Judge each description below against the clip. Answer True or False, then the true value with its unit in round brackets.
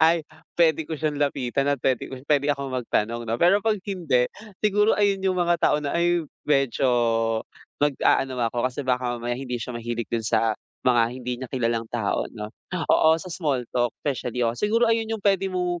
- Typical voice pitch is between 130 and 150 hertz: True (140 Hz)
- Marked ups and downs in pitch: True (6.1 semitones)